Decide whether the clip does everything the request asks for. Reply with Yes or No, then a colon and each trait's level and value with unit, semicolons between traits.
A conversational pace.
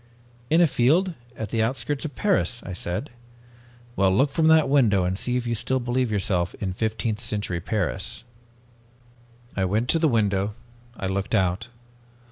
Yes: average, 170 wpm